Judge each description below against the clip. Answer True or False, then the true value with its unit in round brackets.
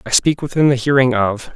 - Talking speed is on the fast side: True (230 wpm)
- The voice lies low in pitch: True (130 Hz)